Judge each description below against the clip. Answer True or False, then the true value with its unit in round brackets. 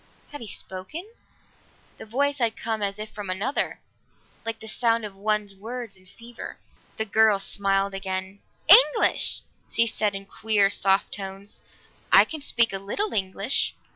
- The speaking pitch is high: True (210 Hz)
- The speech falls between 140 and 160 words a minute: True (155 wpm)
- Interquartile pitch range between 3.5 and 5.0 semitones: False (2.8 semitones)